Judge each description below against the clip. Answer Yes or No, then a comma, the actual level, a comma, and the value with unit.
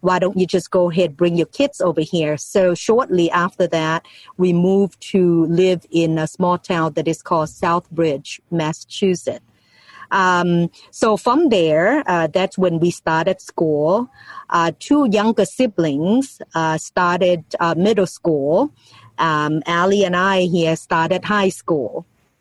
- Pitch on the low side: No, medium, 175 Hz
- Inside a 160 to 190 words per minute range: No, average, 145 wpm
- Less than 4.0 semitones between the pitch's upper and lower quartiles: Yes, narrow, 2.5 semitones